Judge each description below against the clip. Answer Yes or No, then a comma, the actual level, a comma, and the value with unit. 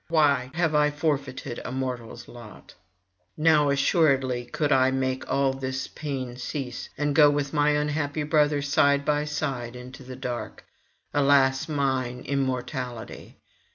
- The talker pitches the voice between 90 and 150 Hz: Yes, medium, 140 Hz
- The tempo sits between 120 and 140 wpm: Yes, slow, 135 wpm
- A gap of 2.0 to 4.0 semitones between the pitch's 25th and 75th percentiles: Yes, narrow, 2.4 semitones